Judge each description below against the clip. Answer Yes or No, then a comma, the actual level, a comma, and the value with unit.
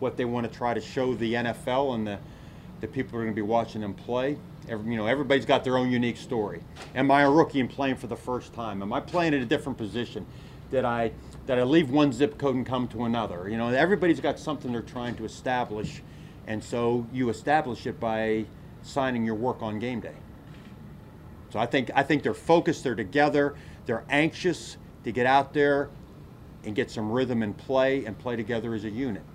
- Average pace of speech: No, fast, 220 wpm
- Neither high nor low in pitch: No, low, 125 Hz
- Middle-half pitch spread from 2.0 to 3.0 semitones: No, average, 3.5 semitones